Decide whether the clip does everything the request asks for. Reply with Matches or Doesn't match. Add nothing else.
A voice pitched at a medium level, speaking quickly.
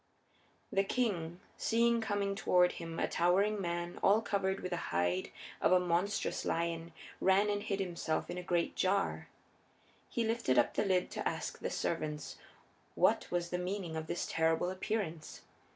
Doesn't match